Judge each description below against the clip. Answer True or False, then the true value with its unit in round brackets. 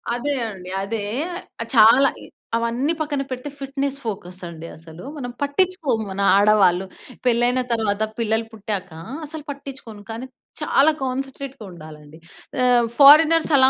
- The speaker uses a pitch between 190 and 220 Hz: False (240 Hz)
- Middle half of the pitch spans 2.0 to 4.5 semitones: False (5.3 semitones)